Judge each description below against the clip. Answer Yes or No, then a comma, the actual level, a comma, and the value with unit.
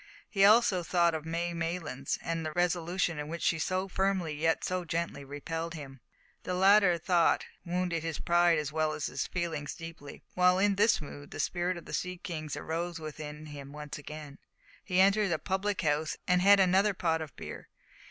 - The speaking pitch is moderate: Yes, medium, 170 Hz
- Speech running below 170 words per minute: No, average, 190 wpm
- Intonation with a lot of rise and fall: No, average, 2.8 semitones